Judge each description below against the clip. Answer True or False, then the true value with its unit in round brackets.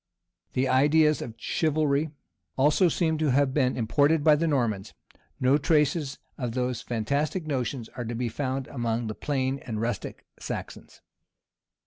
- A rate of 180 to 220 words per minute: False (150 wpm)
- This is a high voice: False (135 Hz)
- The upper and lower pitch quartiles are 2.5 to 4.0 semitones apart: True (3.7 semitones)